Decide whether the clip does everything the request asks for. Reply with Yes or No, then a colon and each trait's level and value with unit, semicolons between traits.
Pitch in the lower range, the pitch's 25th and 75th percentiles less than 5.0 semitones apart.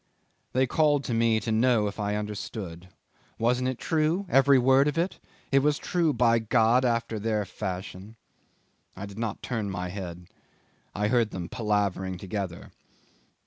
Yes: low, 110 Hz; average, 4.2 semitones